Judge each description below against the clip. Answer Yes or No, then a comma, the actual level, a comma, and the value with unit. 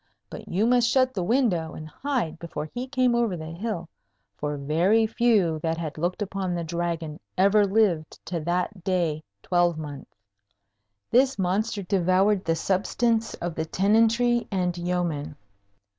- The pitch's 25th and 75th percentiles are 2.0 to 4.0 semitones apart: No, average, 5.1 semitones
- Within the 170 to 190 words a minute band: No, average, 145 wpm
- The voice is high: No, medium, 180 Hz